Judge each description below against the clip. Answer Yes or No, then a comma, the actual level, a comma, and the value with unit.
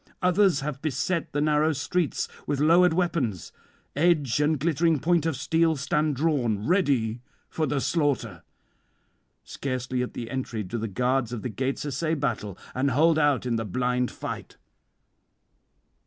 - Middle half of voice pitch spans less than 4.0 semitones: No, average, 4.3 semitones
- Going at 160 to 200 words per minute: No, average, 150 wpm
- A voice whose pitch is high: No, medium, 140 Hz